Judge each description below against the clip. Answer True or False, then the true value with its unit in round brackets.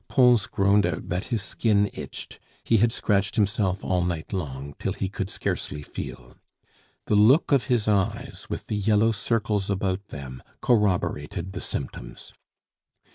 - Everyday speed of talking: True (150 wpm)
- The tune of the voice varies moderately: True (3.2 semitones)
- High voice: False (100 Hz)